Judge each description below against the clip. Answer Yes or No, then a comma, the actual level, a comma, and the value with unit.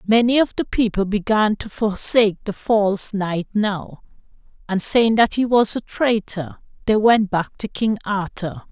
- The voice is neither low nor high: No, high, 210 Hz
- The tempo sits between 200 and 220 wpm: No, average, 165 wpm